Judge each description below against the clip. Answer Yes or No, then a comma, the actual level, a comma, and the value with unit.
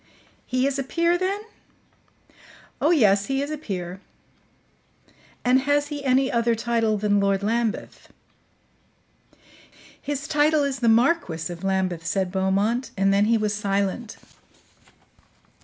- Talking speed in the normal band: No, slow, 130 wpm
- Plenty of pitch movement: Yes, wide, 5.9 semitones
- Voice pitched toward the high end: Yes, high, 230 Hz